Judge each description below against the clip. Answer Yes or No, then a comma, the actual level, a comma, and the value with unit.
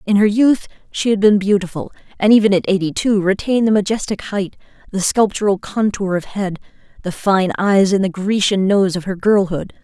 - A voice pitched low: No, high, 200 Hz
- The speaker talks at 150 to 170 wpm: No, average, 190 wpm